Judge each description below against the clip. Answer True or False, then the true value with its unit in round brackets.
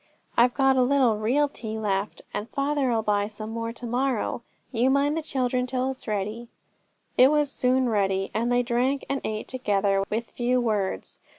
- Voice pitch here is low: False (240 Hz)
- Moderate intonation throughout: True (3.5 semitones)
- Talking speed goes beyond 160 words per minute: True (185 wpm)